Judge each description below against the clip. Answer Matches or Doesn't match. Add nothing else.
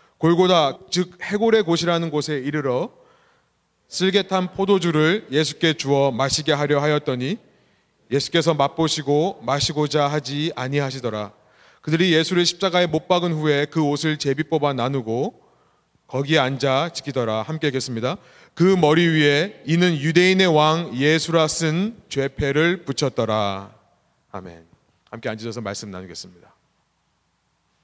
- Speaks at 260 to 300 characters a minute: Matches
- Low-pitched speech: Doesn't match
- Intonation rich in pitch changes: Doesn't match